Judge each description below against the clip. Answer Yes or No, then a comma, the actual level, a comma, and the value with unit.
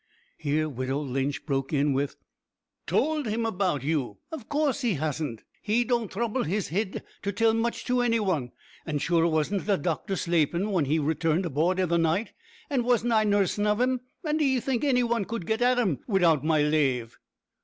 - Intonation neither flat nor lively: No, wide, 7.3 semitones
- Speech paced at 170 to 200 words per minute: Yes, average, 190 wpm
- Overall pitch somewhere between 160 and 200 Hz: Yes, medium, 185 Hz